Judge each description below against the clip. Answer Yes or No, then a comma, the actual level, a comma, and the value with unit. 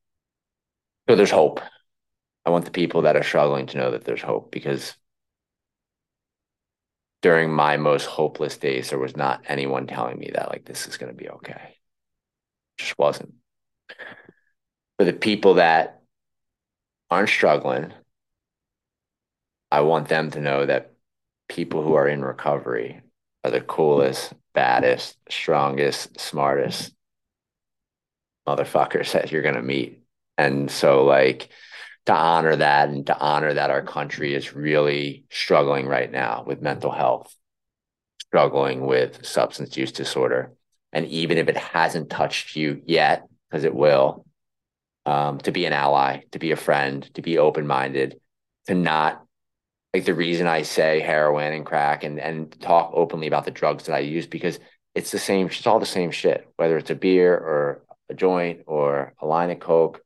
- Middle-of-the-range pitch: No, very low, 75 Hz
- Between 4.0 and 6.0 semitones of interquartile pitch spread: No, average, 3.0 semitones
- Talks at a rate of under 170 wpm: Yes, average, 155 wpm